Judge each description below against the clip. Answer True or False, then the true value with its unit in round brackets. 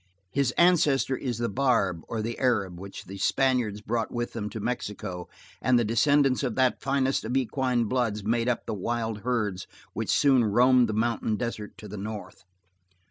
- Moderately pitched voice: False (115 Hz)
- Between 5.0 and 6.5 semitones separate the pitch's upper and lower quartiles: False (3.4 semitones)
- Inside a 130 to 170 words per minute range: False (180 wpm)